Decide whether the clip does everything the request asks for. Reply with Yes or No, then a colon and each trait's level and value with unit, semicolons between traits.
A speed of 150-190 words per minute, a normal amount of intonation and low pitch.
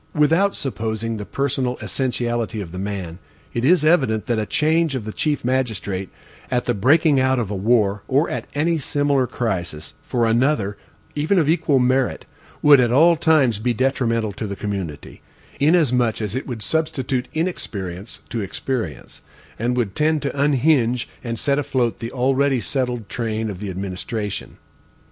Yes: average, 160 wpm; average, 4.7 semitones; low, 125 Hz